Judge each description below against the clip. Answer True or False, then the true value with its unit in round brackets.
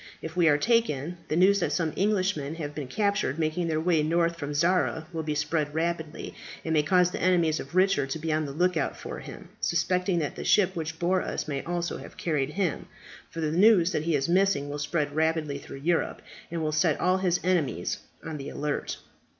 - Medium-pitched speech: True (165 Hz)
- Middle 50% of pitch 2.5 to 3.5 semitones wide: True (3.1 semitones)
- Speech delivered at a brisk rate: True (215 wpm)